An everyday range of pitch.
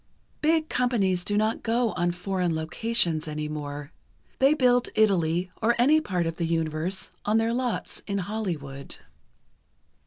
No: wide, 6.1 semitones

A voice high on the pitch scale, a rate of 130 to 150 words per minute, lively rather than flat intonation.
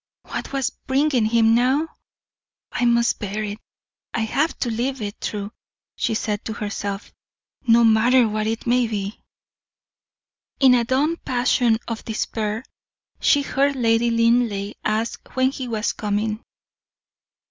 No: high, 230 Hz; slow, 135 wpm; average, 2.8 semitones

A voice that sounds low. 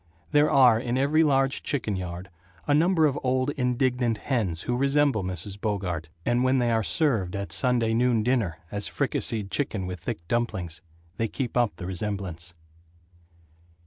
Yes: low, 115 Hz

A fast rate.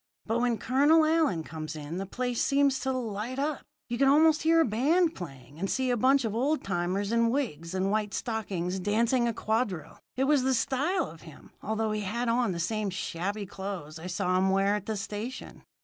Yes: fast, 210 wpm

